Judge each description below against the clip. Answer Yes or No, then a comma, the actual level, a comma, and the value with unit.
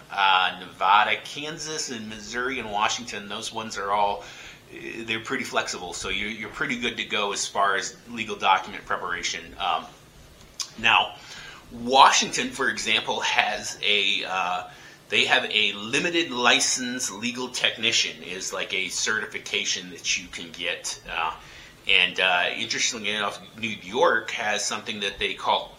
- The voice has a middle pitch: No, low, 110 Hz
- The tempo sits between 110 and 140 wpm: Yes, slow, 135 wpm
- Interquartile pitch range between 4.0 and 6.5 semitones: Yes, average, 4.3 semitones